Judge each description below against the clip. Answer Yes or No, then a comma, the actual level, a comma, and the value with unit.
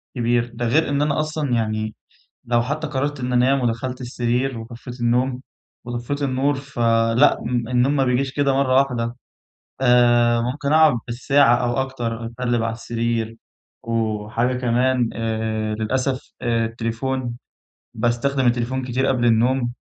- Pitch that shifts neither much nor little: No, narrow, 2.2 semitones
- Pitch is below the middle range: Yes, low, 120 Hz